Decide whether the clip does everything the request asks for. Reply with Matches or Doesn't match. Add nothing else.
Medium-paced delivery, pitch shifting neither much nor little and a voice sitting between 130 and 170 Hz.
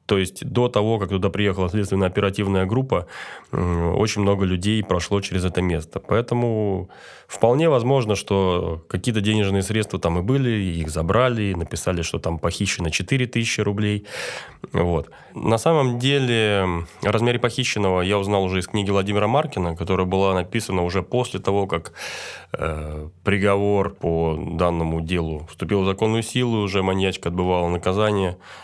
Doesn't match